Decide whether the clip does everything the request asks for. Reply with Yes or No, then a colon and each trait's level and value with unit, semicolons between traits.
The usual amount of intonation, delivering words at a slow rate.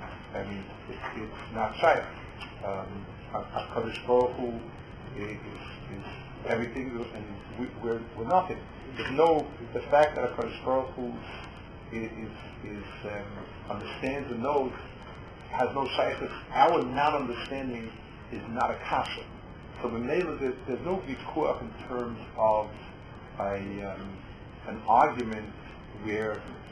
Yes: average, 3.0 semitones; slow, 125 wpm